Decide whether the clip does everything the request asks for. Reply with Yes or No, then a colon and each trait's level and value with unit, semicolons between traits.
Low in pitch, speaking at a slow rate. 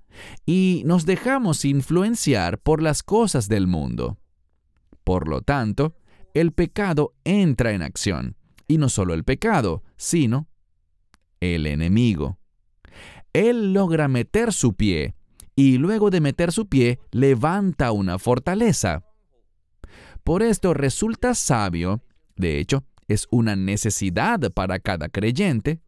Yes: low, 125 Hz; slow, 120 wpm